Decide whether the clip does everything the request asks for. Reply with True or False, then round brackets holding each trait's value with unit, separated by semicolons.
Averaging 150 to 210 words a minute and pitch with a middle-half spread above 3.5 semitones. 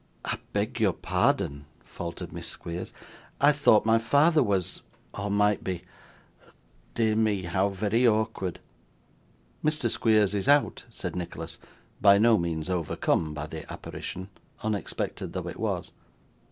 False (135 wpm; 4.2 semitones)